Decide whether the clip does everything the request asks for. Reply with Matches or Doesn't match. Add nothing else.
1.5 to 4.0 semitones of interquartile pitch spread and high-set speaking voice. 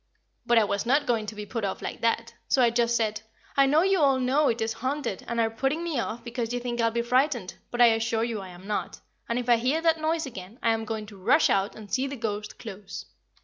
Matches